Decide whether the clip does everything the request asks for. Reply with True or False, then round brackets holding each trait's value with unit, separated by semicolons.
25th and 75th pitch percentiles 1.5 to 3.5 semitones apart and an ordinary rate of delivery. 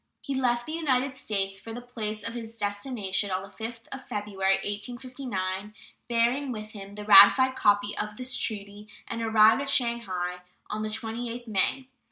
True (3.2 semitones; 170 wpm)